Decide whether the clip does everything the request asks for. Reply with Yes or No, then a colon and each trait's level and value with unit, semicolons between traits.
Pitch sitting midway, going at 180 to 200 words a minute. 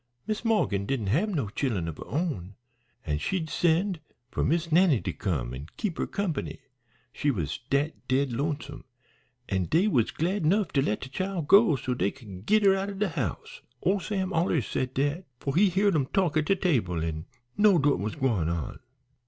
Yes: medium, 150 Hz; average, 195 wpm